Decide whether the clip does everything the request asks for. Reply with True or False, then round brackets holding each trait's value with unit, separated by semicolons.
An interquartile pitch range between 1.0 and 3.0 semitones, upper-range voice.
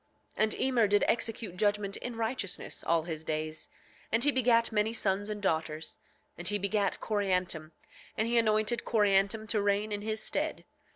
True (2.7 semitones; 205 Hz)